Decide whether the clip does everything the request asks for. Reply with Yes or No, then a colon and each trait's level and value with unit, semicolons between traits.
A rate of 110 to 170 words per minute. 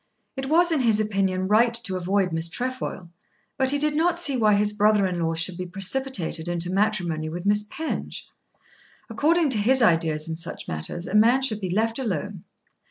No: average, 190 wpm